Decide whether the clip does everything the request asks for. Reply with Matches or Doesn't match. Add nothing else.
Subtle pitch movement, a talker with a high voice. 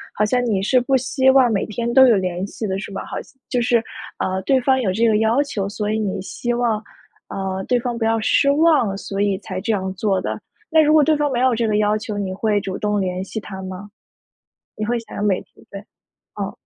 Doesn't match